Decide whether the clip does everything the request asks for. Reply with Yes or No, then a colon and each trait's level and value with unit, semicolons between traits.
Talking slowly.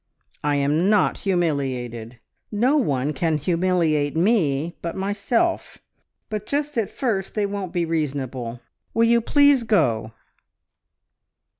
Yes: slow, 120 wpm